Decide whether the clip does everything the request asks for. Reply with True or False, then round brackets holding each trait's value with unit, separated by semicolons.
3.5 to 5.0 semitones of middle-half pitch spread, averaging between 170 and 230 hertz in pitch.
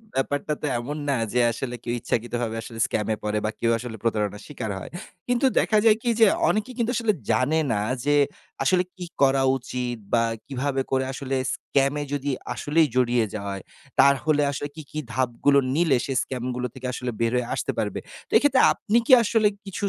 False (4.2 semitones; 135 Hz)